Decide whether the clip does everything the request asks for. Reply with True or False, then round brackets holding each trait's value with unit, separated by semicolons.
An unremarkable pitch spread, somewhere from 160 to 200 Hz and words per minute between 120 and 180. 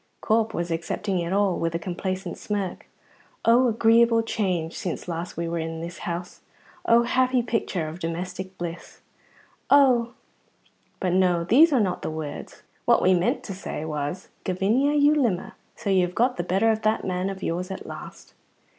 True (4.7 semitones; 185 Hz; 175 wpm)